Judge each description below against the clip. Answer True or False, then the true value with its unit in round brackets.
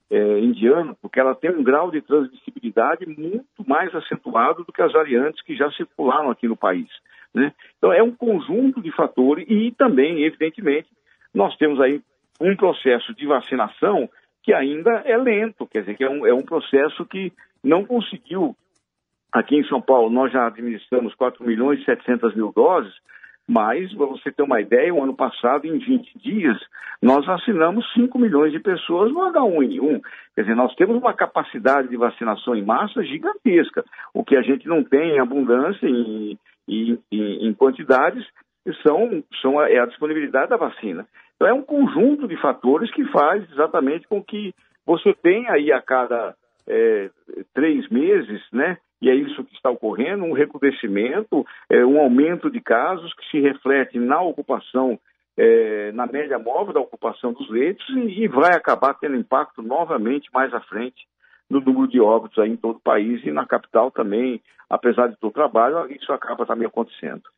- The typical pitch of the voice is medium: True (150 Hz)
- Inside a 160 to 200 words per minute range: True (175 wpm)